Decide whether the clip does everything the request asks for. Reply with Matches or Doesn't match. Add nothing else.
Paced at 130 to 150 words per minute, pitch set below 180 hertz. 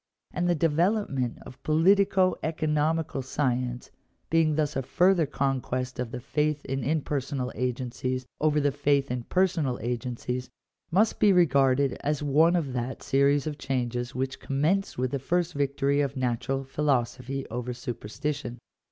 Matches